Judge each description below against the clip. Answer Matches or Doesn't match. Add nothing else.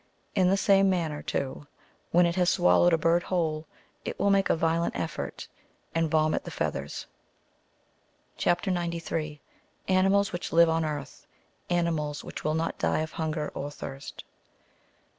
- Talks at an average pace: Matches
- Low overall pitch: Doesn't match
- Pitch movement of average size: Doesn't match